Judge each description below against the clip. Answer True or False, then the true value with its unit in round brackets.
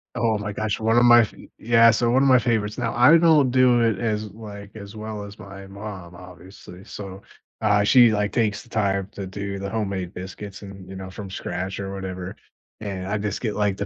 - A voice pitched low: True (105 Hz)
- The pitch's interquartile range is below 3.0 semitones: True (2.6 semitones)